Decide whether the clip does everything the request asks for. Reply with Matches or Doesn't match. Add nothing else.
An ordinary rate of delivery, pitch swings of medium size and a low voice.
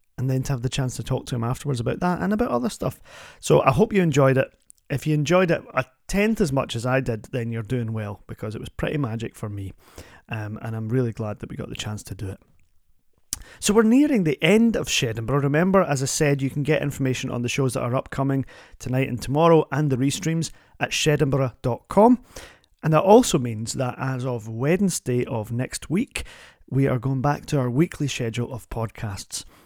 Doesn't match